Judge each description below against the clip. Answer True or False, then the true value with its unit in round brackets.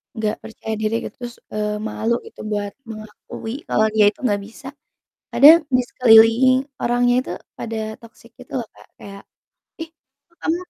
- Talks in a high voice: True (225 Hz)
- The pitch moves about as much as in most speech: False (2.3 semitones)